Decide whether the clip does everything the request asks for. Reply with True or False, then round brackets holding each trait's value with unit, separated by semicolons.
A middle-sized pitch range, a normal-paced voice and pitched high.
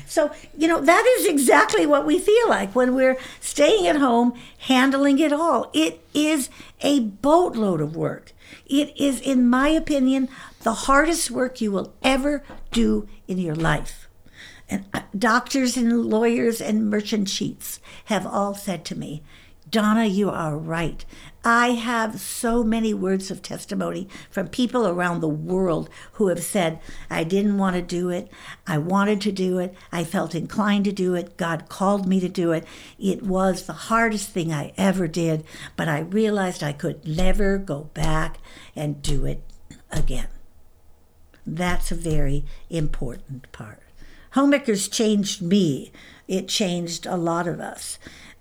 False (6.6 semitones; 155 wpm; 195 Hz)